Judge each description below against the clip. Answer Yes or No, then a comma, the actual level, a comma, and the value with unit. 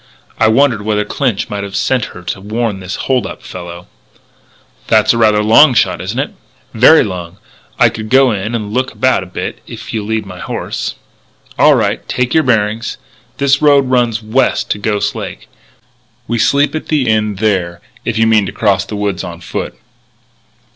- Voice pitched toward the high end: No, low, 110 Hz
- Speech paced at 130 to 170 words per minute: No, average, 185 wpm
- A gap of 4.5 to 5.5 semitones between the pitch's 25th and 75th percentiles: No, average, 3.8 semitones